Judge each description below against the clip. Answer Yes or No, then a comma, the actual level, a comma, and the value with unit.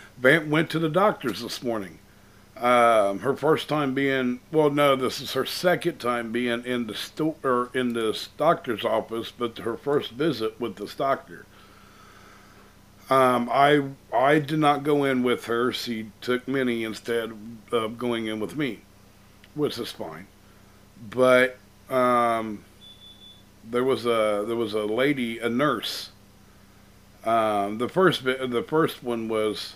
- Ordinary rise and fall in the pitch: Yes, average, 3.9 semitones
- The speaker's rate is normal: Yes, average, 150 wpm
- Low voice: Yes, low, 120 Hz